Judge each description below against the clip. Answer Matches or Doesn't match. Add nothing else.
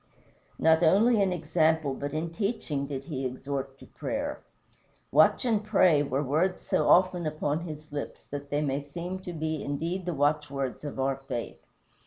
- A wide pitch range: Doesn't match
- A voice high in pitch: Doesn't match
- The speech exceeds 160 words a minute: Matches